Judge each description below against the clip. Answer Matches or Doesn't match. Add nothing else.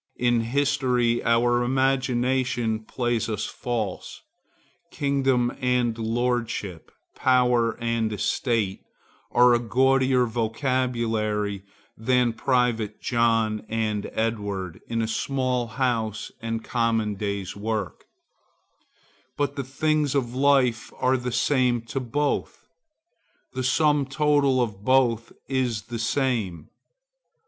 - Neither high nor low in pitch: Doesn't match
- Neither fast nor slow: Doesn't match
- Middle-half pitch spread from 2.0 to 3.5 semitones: Matches